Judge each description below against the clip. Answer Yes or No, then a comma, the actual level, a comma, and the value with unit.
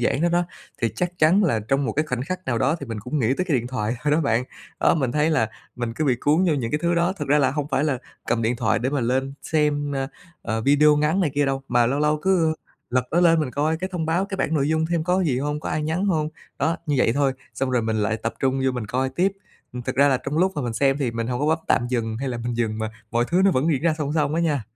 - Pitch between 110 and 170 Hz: Yes, medium, 140 Hz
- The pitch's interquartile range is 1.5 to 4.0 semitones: No, average, 4.4 semitones